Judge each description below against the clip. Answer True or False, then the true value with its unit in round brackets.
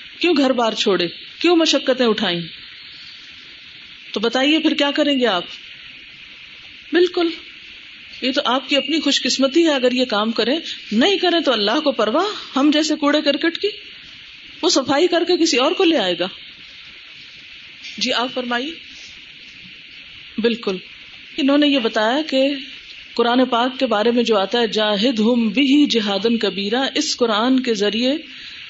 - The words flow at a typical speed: True (155 wpm)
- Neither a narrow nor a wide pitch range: True (4.4 semitones)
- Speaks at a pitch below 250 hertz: False (265 Hz)